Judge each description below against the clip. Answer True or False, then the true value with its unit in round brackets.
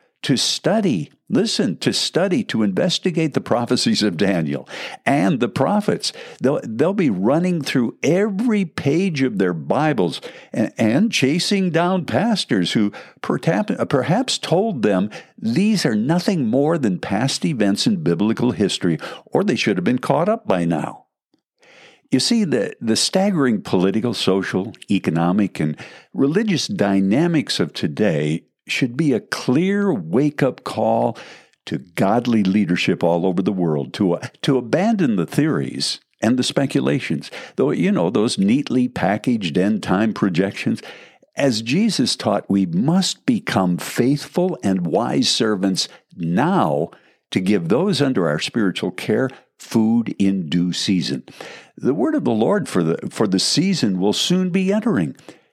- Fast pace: False (145 wpm)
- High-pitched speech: False (135 Hz)